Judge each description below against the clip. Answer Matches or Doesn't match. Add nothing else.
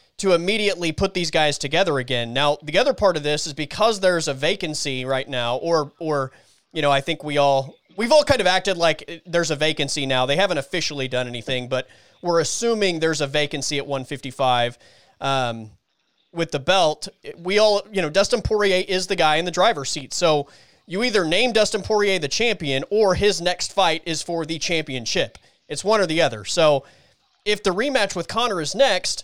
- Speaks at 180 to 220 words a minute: Matches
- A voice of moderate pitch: Matches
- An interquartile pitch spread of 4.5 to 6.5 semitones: Matches